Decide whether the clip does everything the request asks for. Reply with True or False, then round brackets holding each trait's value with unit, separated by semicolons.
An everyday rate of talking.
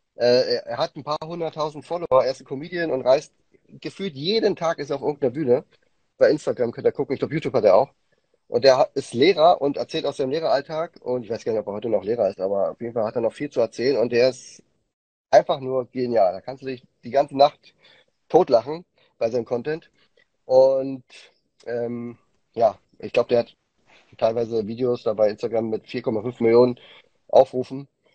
False (200 wpm)